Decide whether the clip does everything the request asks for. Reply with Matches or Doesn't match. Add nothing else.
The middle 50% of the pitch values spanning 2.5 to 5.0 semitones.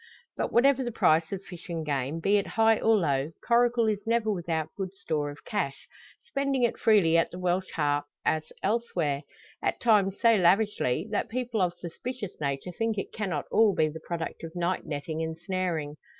Doesn't match